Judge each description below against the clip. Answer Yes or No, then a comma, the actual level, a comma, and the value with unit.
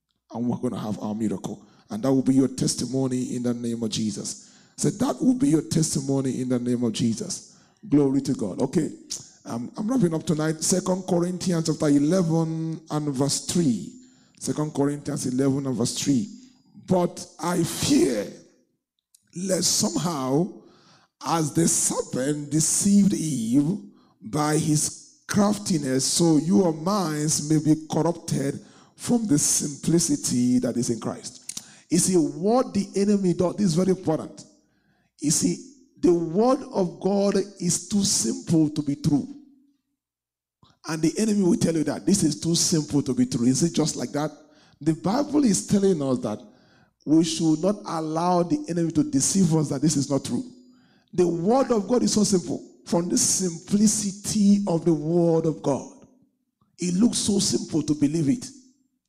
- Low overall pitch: No, medium, 165 Hz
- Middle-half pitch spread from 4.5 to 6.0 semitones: Yes, average, 5.3 semitones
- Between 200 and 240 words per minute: No, average, 160 wpm